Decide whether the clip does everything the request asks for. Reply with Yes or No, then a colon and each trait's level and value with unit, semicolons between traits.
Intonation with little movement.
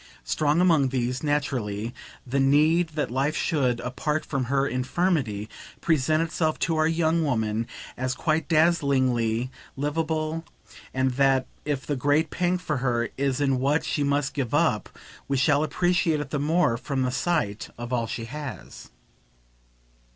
No: average, 3.6 semitones